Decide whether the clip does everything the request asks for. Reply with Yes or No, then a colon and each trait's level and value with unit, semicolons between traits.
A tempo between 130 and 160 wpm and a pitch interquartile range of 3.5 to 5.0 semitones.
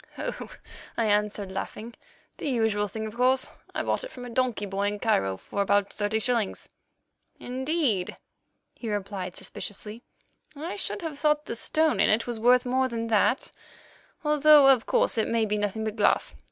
No: average, 175 wpm; average, 3.9 semitones